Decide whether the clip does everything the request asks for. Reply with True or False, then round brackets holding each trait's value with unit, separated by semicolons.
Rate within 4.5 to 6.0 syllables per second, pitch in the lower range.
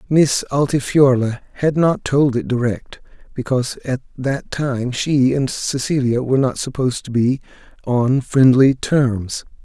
False (4.1 syllables/s; 130 Hz)